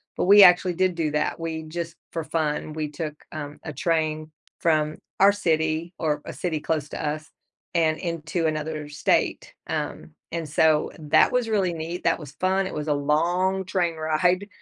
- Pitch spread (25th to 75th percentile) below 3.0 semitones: Yes, narrow, 2.5 semitones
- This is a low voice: No, medium, 160 Hz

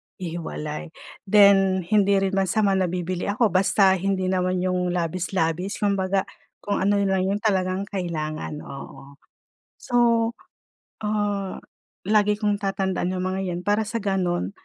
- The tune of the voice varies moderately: No, narrow, 2.0 semitones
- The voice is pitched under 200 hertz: Yes, high, 190 Hz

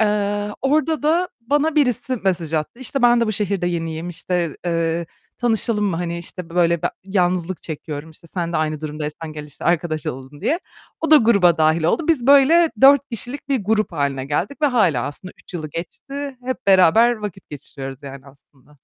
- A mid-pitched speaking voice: Yes, medium, 180 Hz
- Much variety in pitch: Yes, wide, 7.3 semitones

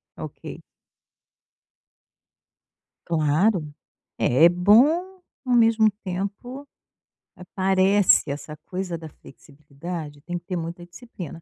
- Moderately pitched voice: Yes, medium, 180 Hz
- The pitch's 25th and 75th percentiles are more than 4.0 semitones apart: Yes, average, 4.7 semitones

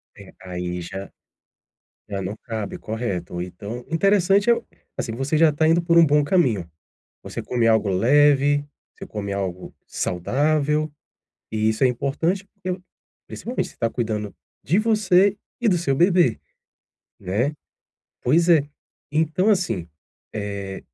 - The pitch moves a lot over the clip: Yes, wide, 8.7 semitones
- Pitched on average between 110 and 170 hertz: Yes, medium, 140 Hz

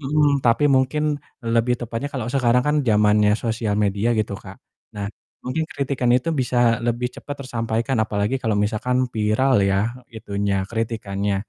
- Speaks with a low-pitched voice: Yes, low, 115 Hz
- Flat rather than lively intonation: No, average, 3.4 semitones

